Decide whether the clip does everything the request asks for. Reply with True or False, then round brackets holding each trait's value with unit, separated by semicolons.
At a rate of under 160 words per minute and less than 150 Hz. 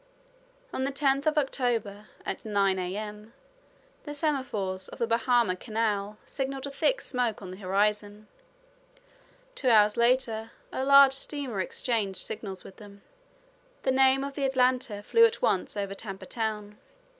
False (145 wpm; 225 Hz)